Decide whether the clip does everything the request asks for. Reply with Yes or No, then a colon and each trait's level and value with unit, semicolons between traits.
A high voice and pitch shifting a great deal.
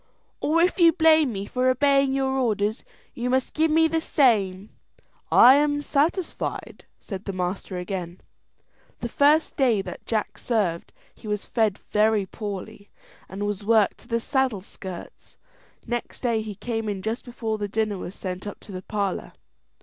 No: high, 220 Hz; average, 4.8 semitones